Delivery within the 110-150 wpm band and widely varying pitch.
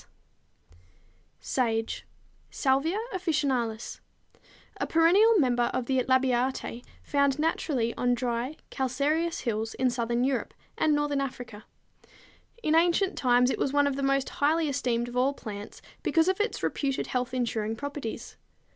No: average, 140 wpm; average, 3.3 semitones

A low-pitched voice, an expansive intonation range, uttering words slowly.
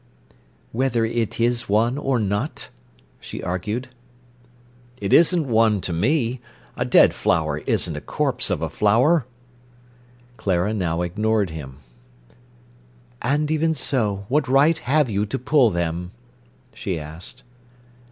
Yes: low, 110 Hz; wide, 6.2 semitones; slow, 125 wpm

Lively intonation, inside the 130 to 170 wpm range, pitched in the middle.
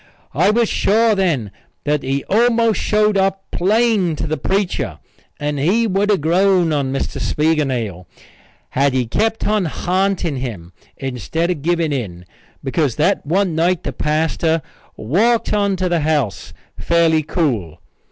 Yes: wide, 5.8 semitones; average, 145 wpm; medium, 165 Hz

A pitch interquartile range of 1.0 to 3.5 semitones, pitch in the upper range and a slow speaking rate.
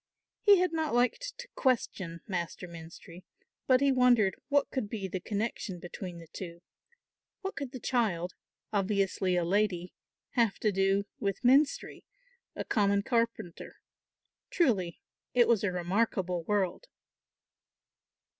No: average, 5.3 semitones; high, 200 Hz; slow, 130 wpm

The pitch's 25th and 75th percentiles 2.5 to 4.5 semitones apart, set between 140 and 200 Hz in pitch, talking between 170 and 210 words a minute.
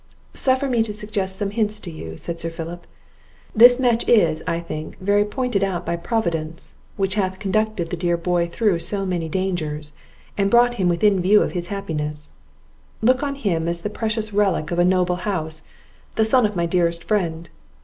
Yes: average, 3.9 semitones; high, 190 Hz; average, 190 wpm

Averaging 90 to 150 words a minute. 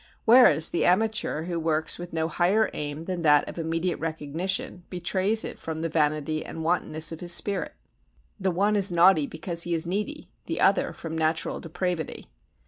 No: average, 175 wpm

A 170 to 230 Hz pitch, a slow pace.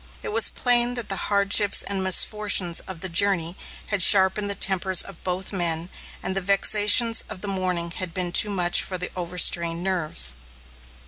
No: high, 190 Hz; average, 175 wpm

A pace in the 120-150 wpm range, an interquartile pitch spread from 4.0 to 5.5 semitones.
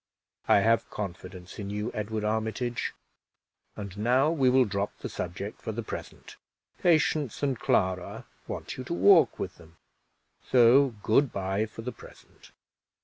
Yes: average, 145 wpm; average, 4.3 semitones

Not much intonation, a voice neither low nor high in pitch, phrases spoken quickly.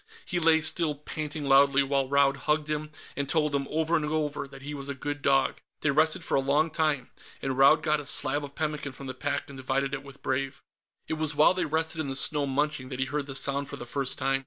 Yes: narrow, 2.0 semitones; medium, 145 Hz; fast, 250 wpm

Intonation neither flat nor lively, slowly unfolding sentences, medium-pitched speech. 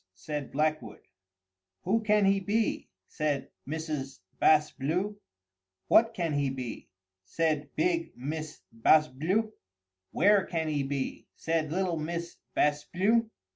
Yes: average, 5.0 semitones; slow, 125 wpm; medium, 155 Hz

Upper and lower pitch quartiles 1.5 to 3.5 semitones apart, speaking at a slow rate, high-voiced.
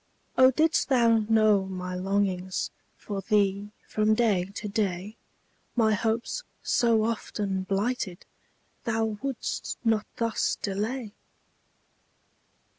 Yes: average, 2.8 semitones; slow, 105 wpm; high, 215 Hz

